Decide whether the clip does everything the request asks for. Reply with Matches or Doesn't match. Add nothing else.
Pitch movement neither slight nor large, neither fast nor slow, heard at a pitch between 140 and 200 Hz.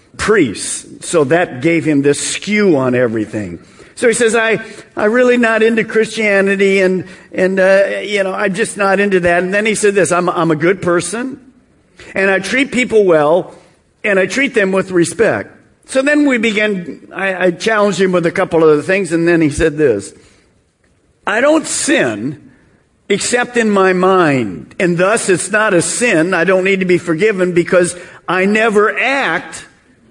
Matches